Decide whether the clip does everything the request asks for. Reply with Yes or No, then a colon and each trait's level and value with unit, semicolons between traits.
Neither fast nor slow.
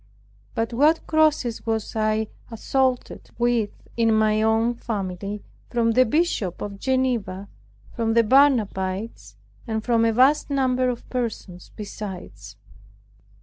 No: slow, 120 wpm